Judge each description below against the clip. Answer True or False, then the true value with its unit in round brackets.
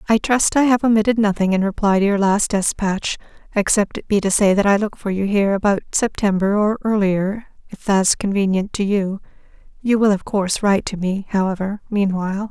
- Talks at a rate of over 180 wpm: True (195 wpm)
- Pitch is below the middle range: False (200 Hz)